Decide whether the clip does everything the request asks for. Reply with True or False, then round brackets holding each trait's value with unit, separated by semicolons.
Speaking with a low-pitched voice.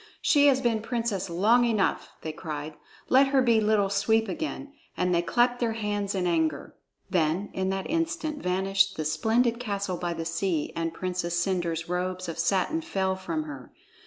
False (195 Hz)